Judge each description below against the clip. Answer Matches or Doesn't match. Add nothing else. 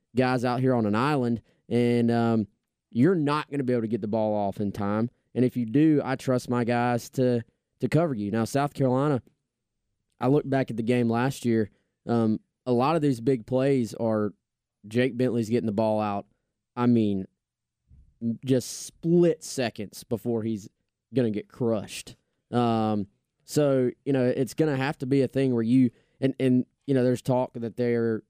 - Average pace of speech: Matches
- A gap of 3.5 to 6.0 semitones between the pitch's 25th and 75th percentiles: Doesn't match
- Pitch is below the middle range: Matches